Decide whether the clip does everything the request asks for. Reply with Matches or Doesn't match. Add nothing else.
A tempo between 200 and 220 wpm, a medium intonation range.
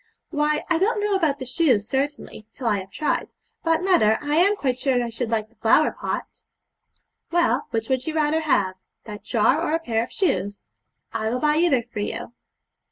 Doesn't match